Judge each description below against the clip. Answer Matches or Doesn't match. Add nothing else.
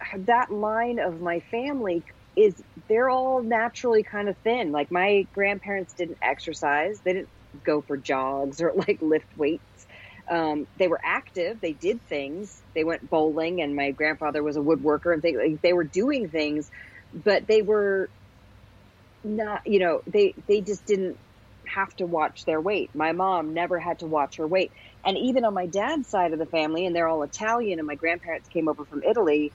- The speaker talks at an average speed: Matches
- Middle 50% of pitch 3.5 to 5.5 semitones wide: Matches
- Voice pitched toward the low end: Doesn't match